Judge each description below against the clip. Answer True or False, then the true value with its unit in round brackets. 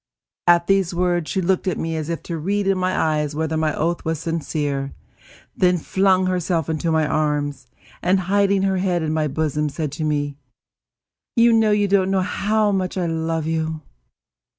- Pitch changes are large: False (3.4 semitones)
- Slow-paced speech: False (175 wpm)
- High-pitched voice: False (170 Hz)